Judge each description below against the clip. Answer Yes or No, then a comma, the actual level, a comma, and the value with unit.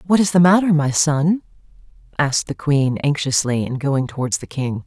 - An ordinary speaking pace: Yes, average, 185 wpm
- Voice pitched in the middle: Yes, medium, 150 Hz